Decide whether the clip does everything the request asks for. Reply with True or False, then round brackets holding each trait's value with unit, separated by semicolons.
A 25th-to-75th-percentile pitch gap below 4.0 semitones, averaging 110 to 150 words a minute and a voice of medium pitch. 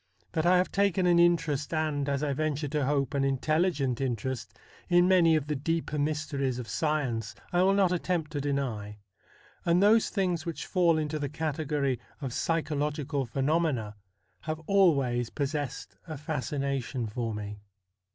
False (3.5 semitones; 160 wpm; 150 Hz)